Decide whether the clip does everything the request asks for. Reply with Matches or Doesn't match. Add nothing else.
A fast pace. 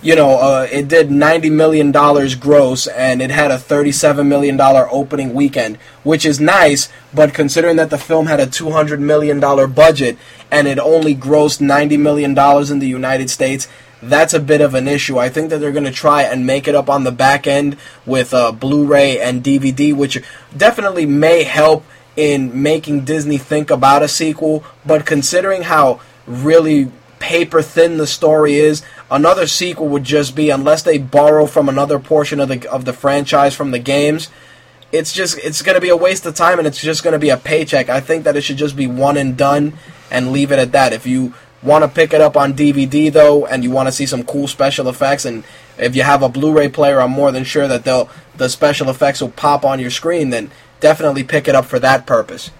Matches